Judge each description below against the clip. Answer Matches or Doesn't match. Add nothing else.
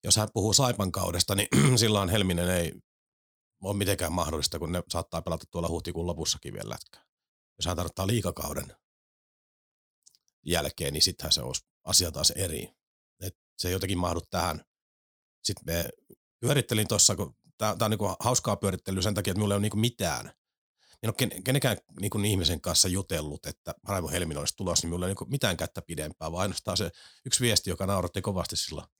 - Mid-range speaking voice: Doesn't match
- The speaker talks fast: Matches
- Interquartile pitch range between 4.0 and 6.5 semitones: Doesn't match